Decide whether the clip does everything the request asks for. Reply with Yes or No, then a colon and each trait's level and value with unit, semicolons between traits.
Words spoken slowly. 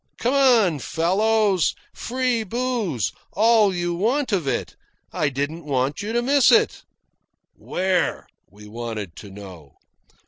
Yes: slow, 130 wpm